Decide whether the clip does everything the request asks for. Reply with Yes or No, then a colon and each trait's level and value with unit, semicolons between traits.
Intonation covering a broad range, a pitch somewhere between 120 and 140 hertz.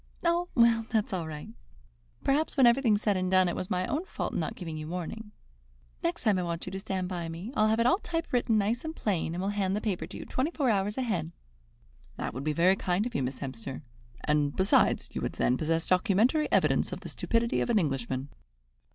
No: wide, 5.8 semitones; high, 195 Hz